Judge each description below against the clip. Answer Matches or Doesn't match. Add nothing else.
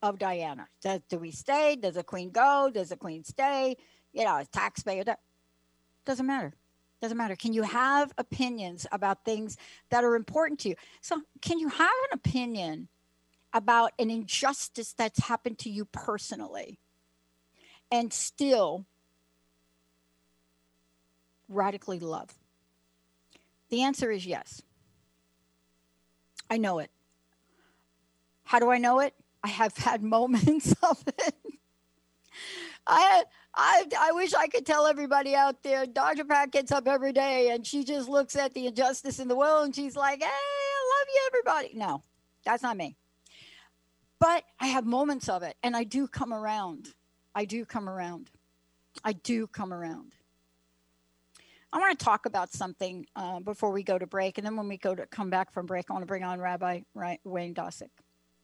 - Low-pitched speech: Doesn't match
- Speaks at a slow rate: Doesn't match